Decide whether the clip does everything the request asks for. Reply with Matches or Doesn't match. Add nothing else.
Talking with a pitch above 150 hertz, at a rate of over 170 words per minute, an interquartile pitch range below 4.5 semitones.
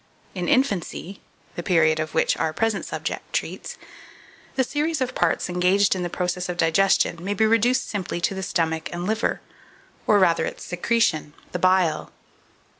Doesn't match